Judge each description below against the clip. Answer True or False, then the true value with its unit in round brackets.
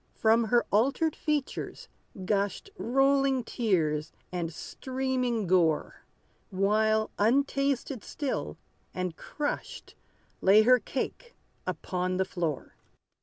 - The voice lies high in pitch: True (220 Hz)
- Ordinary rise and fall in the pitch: False (6.3 semitones)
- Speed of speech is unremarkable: False (95 wpm)